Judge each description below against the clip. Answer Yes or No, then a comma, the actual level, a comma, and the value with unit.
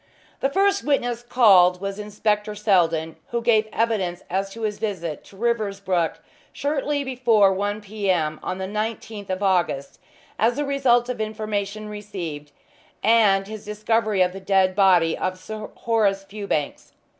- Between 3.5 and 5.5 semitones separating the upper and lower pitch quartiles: No, average, 3.0 semitones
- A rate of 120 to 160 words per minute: Yes, average, 150 wpm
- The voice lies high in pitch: Yes, high, 205 Hz